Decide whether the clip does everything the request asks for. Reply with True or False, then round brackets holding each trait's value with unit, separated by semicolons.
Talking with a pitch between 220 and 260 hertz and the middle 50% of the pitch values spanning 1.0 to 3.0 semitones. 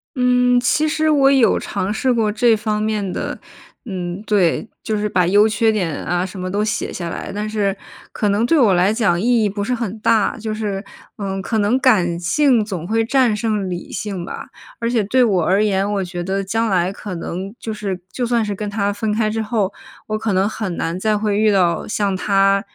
False (210 Hz; 2.7 semitones)